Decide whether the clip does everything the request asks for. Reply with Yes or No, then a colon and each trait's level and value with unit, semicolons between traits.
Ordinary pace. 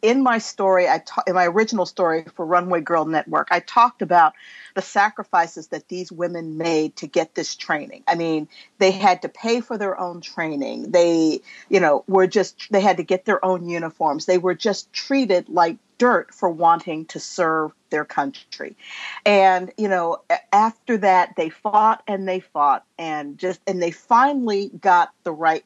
Yes: average, 180 wpm